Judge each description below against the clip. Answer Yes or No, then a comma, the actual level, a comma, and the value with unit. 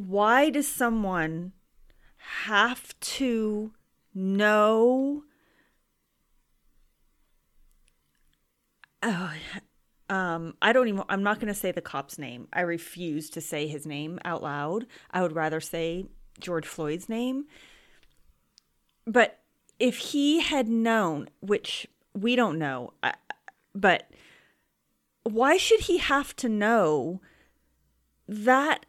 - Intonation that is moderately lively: No, wide, 7.6 semitones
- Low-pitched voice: No, medium, 185 Hz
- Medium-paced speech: No, slow, 105 wpm